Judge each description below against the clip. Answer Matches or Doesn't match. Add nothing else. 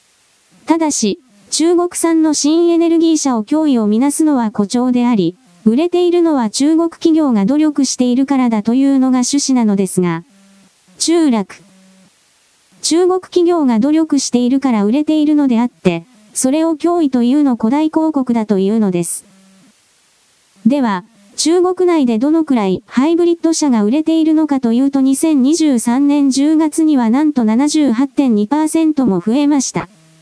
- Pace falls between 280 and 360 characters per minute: Matches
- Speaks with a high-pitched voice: Matches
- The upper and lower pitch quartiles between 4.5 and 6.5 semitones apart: Matches